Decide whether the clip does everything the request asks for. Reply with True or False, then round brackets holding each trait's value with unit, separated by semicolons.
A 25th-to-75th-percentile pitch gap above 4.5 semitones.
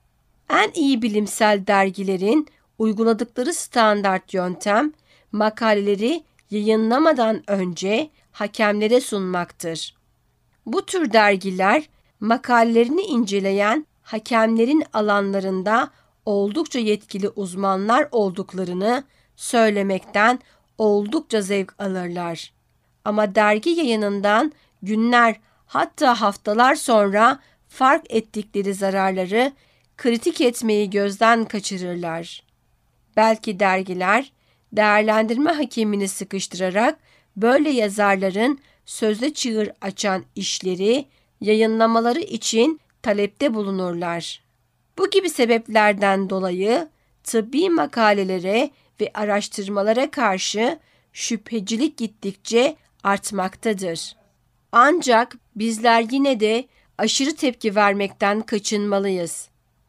False (3.3 semitones)